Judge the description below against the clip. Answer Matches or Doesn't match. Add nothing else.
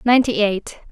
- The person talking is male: Doesn't match